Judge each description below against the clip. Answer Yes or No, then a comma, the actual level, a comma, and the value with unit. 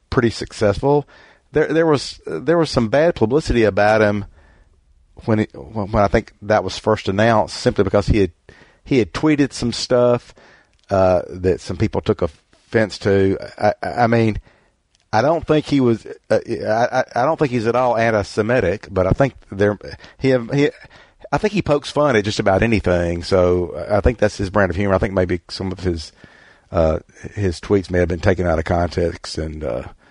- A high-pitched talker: No, low, 105 Hz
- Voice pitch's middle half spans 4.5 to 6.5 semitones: Yes, average, 5.2 semitones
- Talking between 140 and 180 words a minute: No, average, 190 wpm